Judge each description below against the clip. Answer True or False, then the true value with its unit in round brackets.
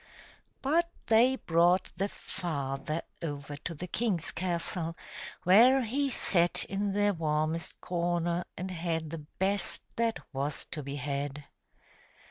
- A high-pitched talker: False (175 Hz)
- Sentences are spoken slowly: True (125 wpm)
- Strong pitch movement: False (4.4 semitones)